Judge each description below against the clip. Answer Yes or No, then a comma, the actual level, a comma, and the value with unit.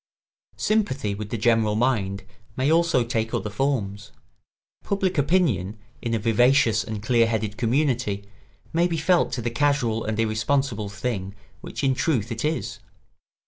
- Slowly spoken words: No, average, 155 wpm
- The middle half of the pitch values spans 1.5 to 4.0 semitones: No, average, 4.8 semitones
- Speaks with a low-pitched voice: Yes, low, 115 Hz